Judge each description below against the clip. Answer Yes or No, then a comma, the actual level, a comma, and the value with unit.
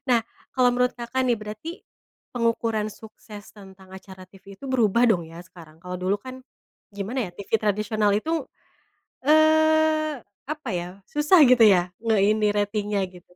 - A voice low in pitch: No, high, 215 Hz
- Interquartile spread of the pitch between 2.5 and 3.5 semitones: No, average, 4.6 semitones